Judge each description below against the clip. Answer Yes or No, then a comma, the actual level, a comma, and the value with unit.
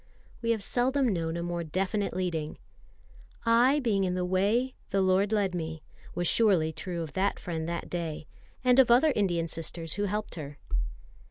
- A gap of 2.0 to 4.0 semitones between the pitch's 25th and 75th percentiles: No, average, 4.5 semitones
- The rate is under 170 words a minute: No, average, 175 wpm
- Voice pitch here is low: No, medium, 185 Hz